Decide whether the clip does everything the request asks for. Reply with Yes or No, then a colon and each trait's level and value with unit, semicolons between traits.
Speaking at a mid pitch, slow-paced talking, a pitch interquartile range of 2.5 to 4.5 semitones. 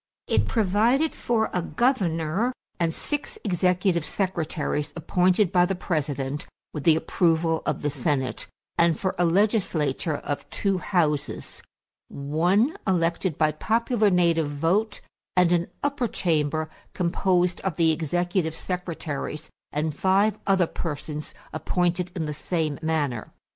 Yes: medium, 170 Hz; slow, 125 wpm; average, 3.6 semitones